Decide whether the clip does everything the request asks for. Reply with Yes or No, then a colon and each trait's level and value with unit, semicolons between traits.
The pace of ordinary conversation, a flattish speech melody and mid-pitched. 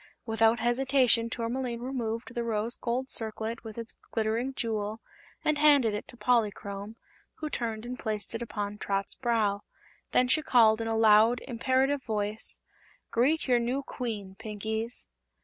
No: average, 150 wpm; narrow, 2.3 semitones; high, 230 Hz